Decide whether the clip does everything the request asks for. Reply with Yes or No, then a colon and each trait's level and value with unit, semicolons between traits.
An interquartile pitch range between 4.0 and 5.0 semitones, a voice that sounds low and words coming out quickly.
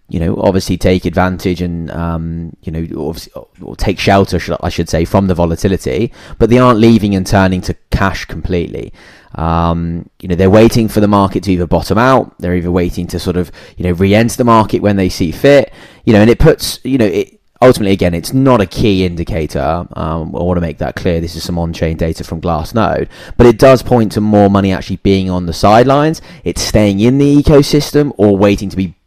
Yes: average, 4.3 semitones; very low, 95 Hz; fast, 215 wpm